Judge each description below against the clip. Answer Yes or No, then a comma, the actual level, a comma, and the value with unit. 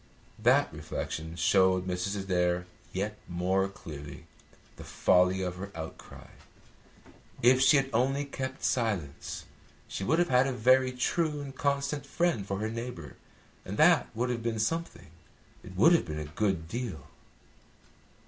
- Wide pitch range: Yes, wide, 6.5 semitones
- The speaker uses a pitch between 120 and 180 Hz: No, low, 105 Hz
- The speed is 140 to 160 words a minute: Yes, average, 150 wpm